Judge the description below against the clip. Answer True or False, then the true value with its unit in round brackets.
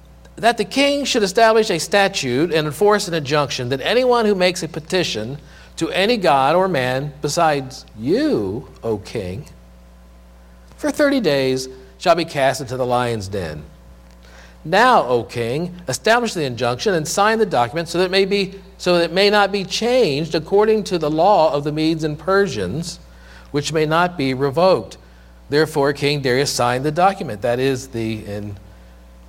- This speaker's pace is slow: False (170 wpm)